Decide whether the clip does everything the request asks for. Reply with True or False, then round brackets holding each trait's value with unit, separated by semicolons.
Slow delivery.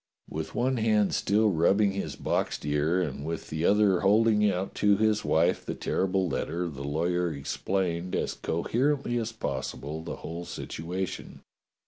False (150 wpm)